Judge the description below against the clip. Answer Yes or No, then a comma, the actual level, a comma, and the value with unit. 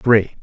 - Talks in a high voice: No, low, 110 Hz